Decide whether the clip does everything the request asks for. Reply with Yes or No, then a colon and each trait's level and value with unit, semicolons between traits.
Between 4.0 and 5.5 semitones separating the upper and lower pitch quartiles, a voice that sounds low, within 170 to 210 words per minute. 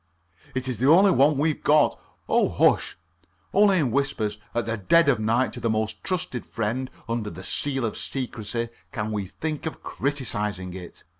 Yes: average, 5.0 semitones; low, 120 Hz; average, 175 wpm